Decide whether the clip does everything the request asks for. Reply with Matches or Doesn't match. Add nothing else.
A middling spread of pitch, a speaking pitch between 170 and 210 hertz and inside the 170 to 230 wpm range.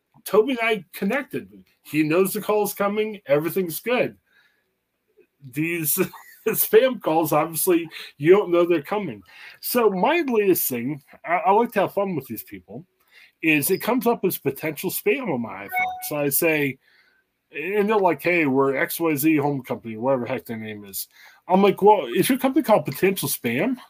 Doesn't match